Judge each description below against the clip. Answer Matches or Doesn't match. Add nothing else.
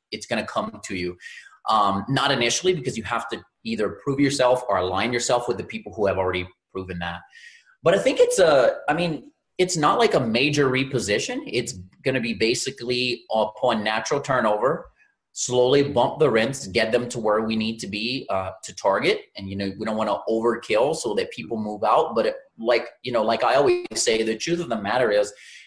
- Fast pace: Matches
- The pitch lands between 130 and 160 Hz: Doesn't match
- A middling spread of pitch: Doesn't match